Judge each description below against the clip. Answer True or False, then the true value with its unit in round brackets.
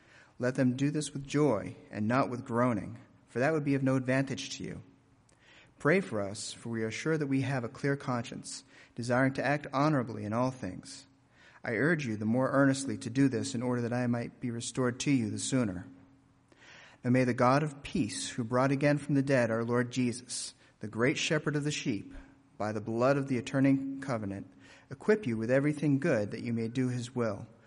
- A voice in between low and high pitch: False (130 Hz)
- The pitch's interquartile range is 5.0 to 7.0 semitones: False (2.8 semitones)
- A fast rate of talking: True (215 wpm)